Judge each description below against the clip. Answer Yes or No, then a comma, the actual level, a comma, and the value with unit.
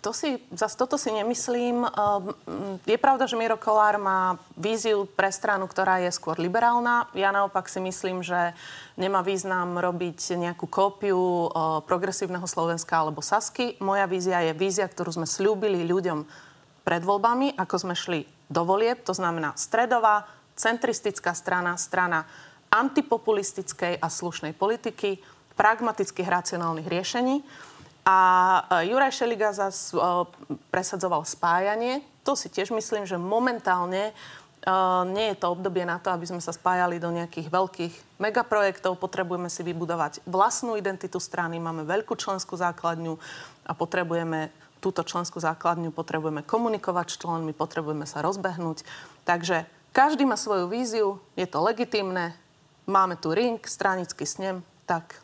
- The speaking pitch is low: No, medium, 185 Hz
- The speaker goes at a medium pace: Yes, average, 135 wpm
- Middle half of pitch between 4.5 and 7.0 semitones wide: No, average, 3.5 semitones